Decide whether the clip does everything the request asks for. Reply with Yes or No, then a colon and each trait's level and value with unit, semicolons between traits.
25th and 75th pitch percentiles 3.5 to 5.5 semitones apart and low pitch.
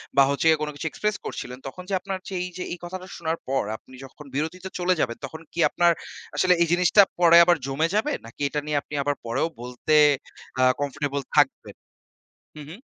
No: average, 4.3 semitones; medium, 160 Hz